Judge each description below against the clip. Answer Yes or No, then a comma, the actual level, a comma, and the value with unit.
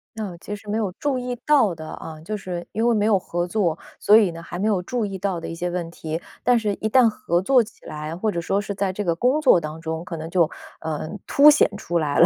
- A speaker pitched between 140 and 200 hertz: Yes, high, 190 Hz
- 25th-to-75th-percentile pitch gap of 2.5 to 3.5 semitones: No, average, 4.5 semitones